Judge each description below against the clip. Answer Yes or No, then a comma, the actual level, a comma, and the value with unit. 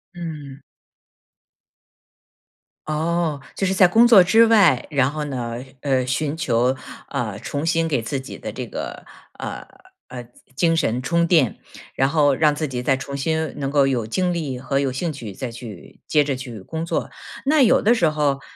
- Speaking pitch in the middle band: Yes, medium, 145 Hz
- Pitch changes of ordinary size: Yes, average, 4.2 semitones